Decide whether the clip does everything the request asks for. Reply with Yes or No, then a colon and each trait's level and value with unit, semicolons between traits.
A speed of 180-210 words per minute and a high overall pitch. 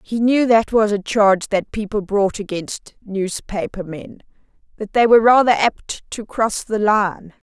No: average, 160 wpm; high, 210 Hz